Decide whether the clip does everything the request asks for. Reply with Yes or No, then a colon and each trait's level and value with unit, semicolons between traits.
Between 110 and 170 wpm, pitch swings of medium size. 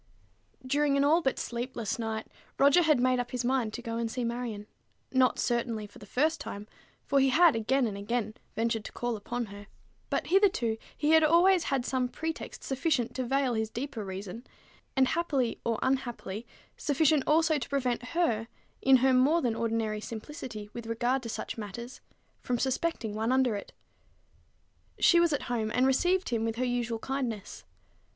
No: average, 180 wpm; average, 3.6 semitones